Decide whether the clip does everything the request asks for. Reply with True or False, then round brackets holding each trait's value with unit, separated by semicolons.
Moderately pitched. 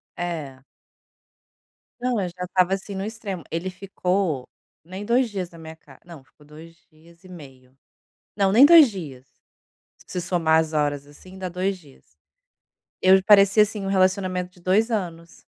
True (180 Hz)